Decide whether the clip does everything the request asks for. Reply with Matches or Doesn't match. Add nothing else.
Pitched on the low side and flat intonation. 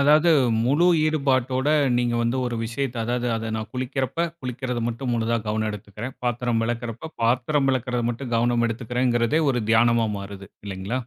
Matches